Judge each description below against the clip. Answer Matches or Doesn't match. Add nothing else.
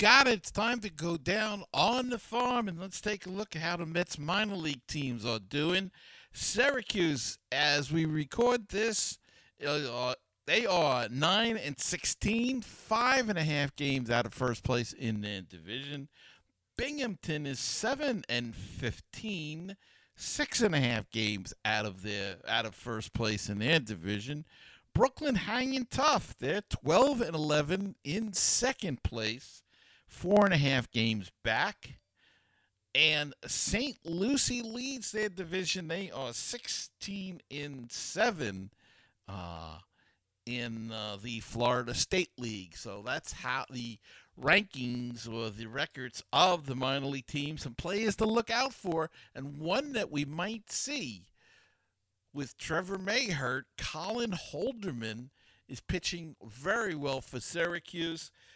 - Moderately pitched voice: Matches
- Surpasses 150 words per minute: Doesn't match